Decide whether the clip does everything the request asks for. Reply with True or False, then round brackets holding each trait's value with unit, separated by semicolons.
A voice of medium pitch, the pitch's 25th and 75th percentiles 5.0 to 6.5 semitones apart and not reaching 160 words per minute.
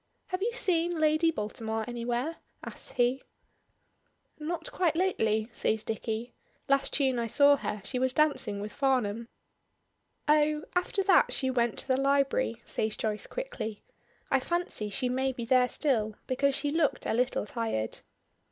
False (260 Hz; 5.3 semitones; 150 wpm)